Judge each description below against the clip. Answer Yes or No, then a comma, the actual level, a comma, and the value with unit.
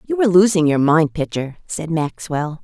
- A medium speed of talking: Yes, average, 185 wpm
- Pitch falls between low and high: Yes, medium, 170 Hz